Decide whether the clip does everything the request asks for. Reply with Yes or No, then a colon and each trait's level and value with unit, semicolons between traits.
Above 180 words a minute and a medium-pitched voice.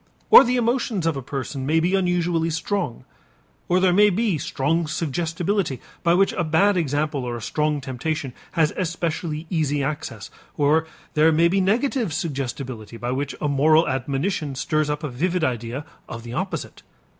No: average, 170 wpm; medium, 155 Hz